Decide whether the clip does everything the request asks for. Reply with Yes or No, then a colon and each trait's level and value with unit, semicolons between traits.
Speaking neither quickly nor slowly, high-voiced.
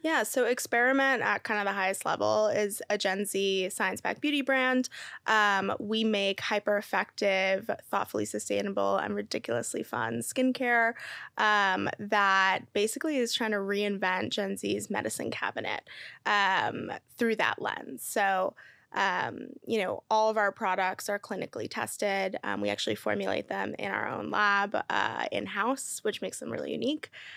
Yes: average, 155 wpm; high, 205 Hz